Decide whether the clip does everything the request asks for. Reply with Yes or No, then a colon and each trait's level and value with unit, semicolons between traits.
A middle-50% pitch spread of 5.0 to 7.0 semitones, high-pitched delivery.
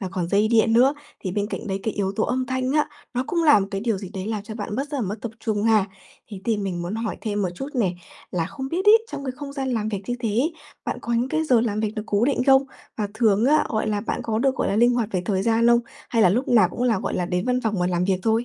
No: average, 3.8 semitones; high, 225 Hz